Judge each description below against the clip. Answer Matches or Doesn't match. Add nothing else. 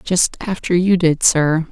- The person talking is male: Doesn't match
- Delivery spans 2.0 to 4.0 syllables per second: Matches